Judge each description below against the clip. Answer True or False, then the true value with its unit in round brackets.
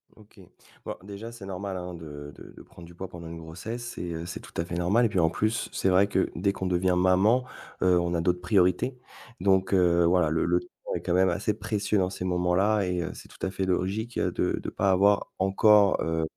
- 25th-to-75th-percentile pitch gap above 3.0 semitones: False (2.5 semitones)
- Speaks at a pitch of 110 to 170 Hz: False (95 Hz)